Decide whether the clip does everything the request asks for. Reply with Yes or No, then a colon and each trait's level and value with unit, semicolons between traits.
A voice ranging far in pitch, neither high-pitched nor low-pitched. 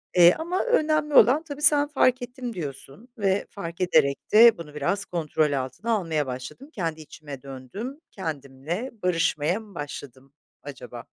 Yes: wide, 9.0 semitones; medium, 175 Hz